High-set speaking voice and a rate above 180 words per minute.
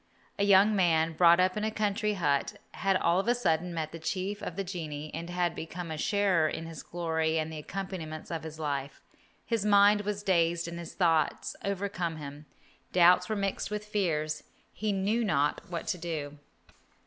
No: medium, 175 Hz; average, 190 wpm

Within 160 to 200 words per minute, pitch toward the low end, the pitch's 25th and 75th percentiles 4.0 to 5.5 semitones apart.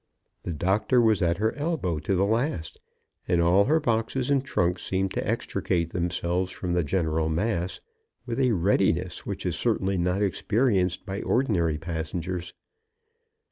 No: average, 150 wpm; very low, 95 Hz; average, 4.5 semitones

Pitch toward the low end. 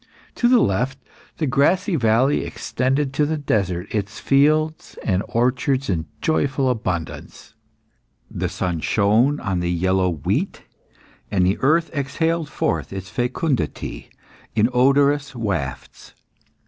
Yes: low, 125 Hz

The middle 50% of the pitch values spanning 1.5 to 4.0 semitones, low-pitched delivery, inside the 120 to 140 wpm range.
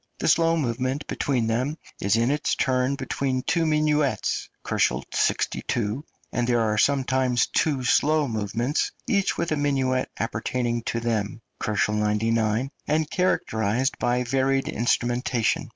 Yes: average, 3.7 semitones; low, 125 Hz; slow, 135 wpm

